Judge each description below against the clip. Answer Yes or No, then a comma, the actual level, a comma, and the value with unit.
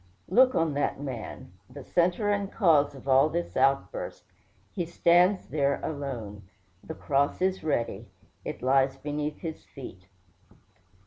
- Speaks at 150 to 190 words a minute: No, slow, 135 wpm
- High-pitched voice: No, medium, 145 Hz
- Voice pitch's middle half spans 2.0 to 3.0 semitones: No, average, 4.2 semitones